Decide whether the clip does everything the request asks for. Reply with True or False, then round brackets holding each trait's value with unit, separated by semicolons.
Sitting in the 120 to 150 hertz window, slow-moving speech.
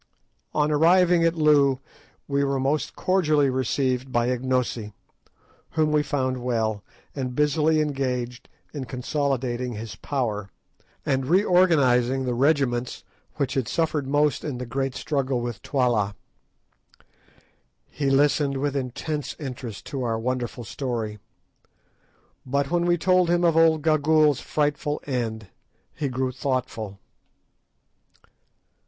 True (135 Hz; 120 wpm)